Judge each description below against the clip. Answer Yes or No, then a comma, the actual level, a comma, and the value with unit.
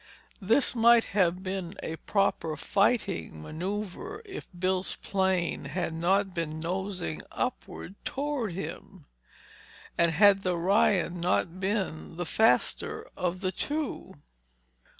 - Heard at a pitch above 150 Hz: Yes, high, 190 Hz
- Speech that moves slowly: Yes, slow, 115 wpm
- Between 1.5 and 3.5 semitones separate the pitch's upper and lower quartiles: Yes, average, 3.1 semitones